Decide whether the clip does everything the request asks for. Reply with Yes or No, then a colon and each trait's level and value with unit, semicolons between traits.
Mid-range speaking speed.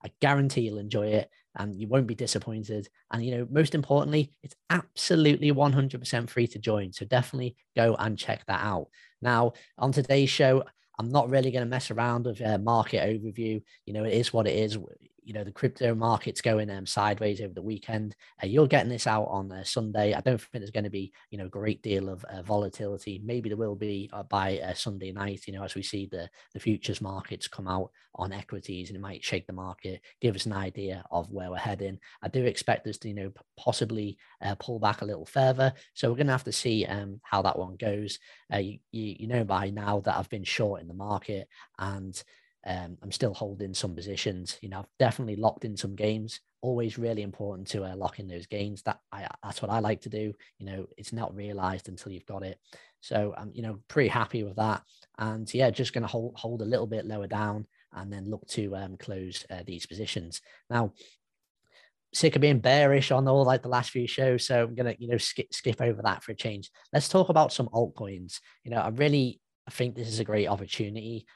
No: fast, 225 wpm